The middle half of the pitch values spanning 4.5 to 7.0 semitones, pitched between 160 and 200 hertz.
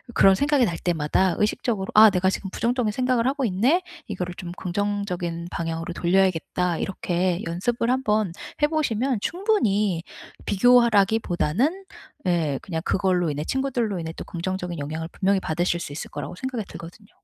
Yes: wide, 5.4 semitones; high, 190 Hz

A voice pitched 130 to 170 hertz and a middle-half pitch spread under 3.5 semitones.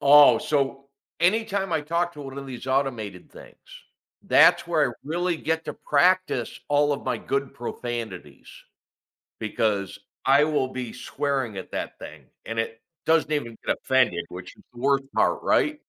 No: low, 135 Hz; average, 4.6 semitones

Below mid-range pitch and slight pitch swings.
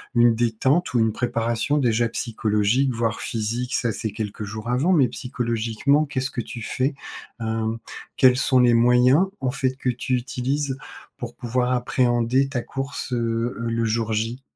Yes: low, 120 Hz; narrow, 2.3 semitones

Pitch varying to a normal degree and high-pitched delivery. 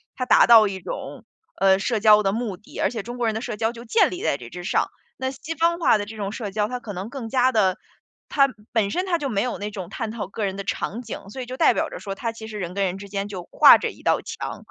Yes: average, 3.6 semitones; high, 215 Hz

